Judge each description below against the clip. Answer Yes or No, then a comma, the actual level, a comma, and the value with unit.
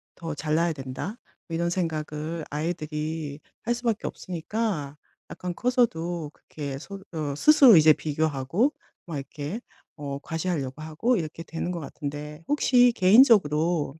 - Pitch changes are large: No, average, 3.6 semitones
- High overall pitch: No, medium, 160 Hz